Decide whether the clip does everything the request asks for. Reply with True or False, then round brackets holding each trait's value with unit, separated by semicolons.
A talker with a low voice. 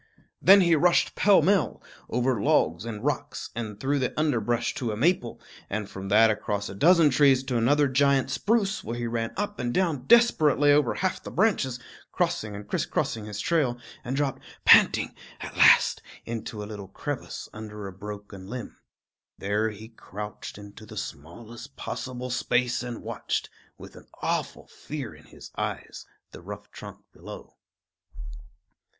True (120 Hz)